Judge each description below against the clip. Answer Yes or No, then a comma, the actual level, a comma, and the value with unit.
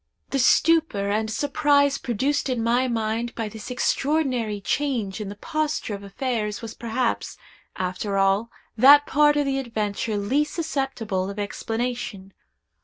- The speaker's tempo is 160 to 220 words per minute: No, average, 140 wpm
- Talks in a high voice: Yes, high, 235 Hz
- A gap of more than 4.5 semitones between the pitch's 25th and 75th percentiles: Yes, average, 4.9 semitones